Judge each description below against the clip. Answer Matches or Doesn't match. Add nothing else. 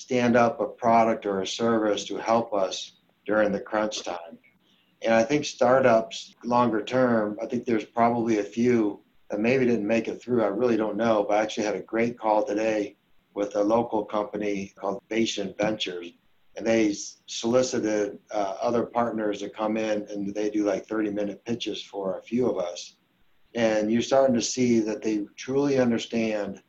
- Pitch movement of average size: Doesn't match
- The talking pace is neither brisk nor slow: Matches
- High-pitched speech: Doesn't match